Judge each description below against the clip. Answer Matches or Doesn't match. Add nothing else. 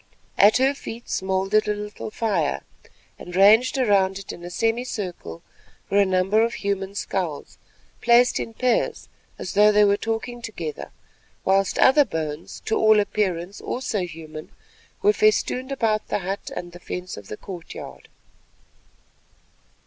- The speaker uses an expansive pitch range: Doesn't match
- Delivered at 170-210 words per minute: Doesn't match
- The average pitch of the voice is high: Matches